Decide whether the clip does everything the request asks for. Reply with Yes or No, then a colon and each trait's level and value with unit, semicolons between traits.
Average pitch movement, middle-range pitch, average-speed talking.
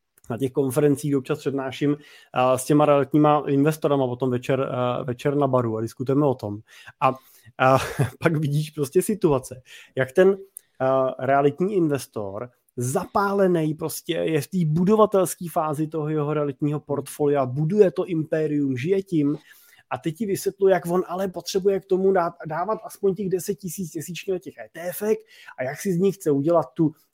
Yes: average, 5.0 semitones; medium, 150 Hz; average, 160 wpm